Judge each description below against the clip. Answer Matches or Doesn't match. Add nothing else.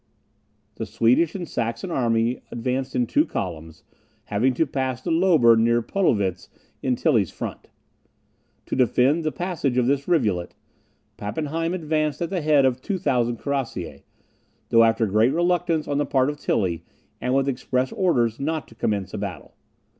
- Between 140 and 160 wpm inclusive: Matches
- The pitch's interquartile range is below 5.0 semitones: Doesn't match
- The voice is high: Doesn't match